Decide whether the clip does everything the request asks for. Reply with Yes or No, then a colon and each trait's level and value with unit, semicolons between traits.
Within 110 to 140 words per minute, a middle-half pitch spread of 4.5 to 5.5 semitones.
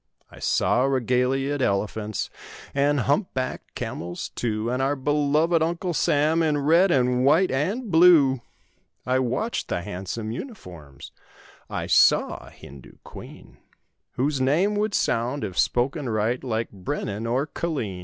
Yes: slow, 135 wpm; average, 5.0 semitones